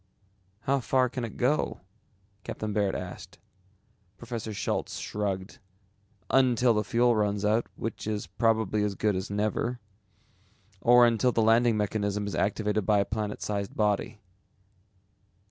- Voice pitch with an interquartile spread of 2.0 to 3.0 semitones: Yes, narrow, 2.4 semitones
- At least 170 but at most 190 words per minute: No, slow, 135 wpm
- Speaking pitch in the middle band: No, low, 110 Hz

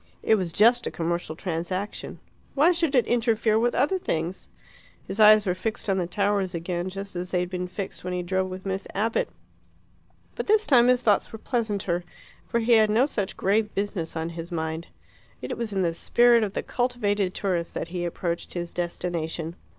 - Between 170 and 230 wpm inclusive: Yes, average, 195 wpm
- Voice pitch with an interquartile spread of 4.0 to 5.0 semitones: Yes, average, 4.3 semitones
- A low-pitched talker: No, high, 195 Hz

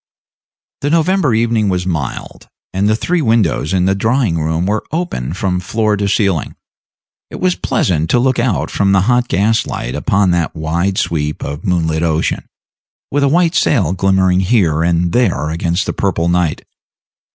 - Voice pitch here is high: No, very low, 95 Hz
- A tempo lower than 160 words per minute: No, average, 170 wpm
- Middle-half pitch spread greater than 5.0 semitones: Yes, wide, 5.4 semitones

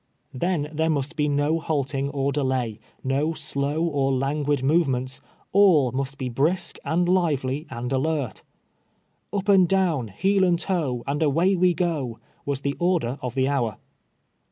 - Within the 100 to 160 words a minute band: Yes, average, 155 wpm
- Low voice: No, medium, 145 Hz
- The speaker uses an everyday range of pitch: Yes, average, 4.0 semitones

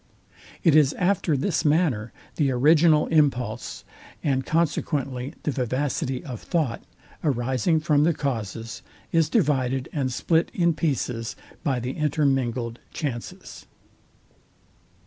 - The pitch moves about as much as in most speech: Yes, average, 3.9 semitones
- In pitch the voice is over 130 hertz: Yes, medium, 140 Hz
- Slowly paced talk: Yes, slow, 110 wpm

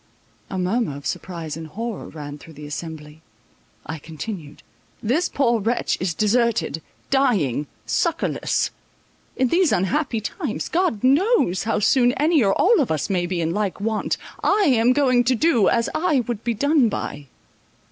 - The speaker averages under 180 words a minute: Yes, average, 155 wpm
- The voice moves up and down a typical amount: No, wide, 7.7 semitones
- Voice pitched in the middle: No, high, 220 Hz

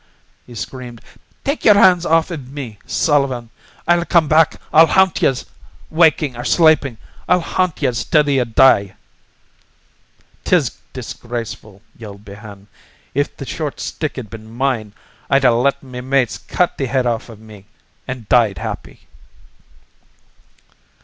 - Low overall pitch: Yes, low, 130 Hz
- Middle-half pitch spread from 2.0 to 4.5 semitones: No, average, 5.2 semitones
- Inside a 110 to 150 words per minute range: Yes, slow, 135 wpm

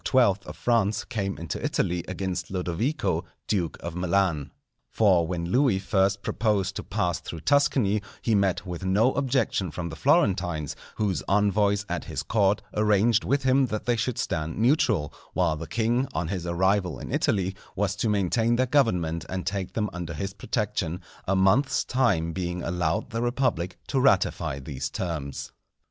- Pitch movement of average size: Yes, average, 4.4 semitones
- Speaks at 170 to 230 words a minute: No, average, 160 wpm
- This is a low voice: Yes, very low, 95 Hz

